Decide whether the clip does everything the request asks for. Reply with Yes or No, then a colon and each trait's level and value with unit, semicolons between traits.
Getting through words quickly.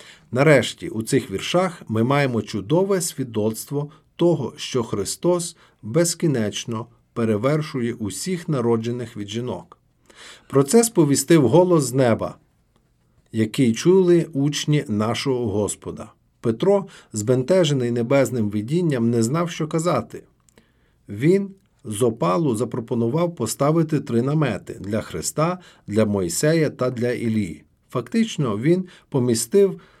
No: slow, 105 wpm